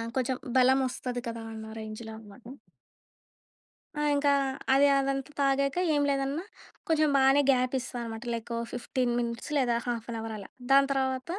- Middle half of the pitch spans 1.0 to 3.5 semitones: Yes, average, 2.9 semitones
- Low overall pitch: No, very high, 255 Hz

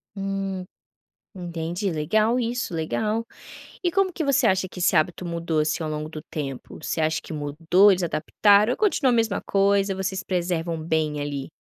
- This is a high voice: No, medium, 180 Hz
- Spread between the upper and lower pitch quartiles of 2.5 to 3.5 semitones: No, average, 4.6 semitones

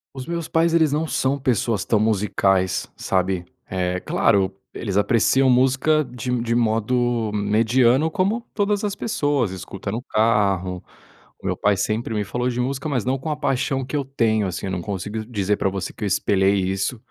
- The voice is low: Yes, low, 115 Hz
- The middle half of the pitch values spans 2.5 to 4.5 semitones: No, average, 5.2 semitones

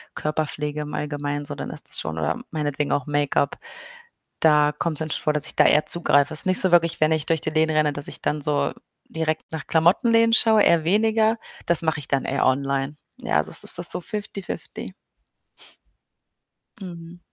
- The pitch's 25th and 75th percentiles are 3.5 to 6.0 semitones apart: No, average, 2.7 semitones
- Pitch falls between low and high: Yes, medium, 155 Hz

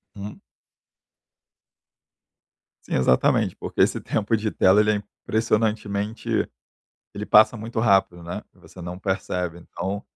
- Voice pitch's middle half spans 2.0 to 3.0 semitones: Yes, average, 2.7 semitones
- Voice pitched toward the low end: Yes, low, 100 Hz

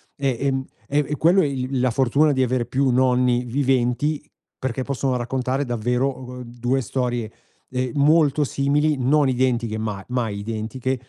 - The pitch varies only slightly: Yes, narrow, 2.1 semitones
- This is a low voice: Yes, low, 130 Hz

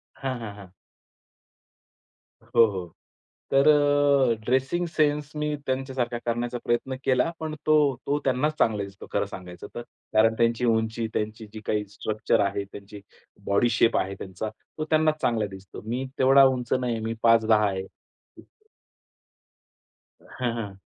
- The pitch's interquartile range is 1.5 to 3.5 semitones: No, average, 3.9 semitones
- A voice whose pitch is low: Yes, low, 120 Hz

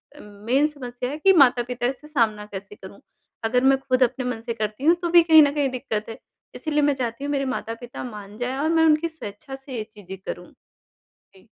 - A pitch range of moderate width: Yes, average, 4.5 semitones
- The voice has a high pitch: Yes, very high, 250 Hz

